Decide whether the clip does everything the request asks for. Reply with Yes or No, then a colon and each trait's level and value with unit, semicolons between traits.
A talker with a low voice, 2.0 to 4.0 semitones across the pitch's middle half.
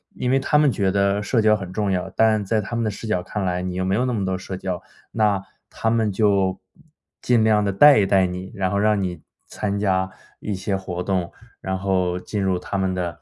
Yes: low, 100 Hz; narrow, 2.4 semitones